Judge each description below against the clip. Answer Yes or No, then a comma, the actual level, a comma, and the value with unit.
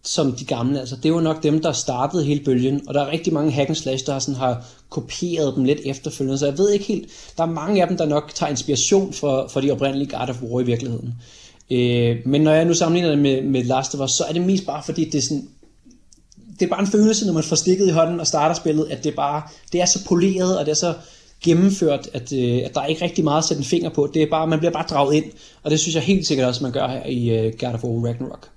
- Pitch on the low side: No, medium, 150 Hz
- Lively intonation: No, average, 3.9 semitones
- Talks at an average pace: No, fast, 280 wpm